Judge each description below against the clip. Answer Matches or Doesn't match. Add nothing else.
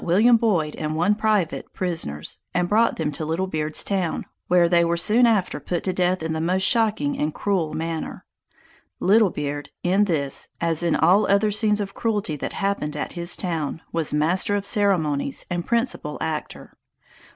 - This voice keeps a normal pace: Matches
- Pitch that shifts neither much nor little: Matches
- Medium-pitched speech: Matches